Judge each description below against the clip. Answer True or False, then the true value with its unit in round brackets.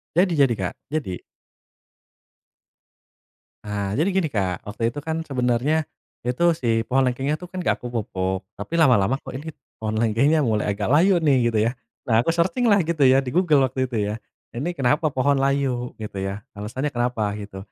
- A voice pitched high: False (130 Hz)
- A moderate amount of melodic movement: False (6.1 semitones)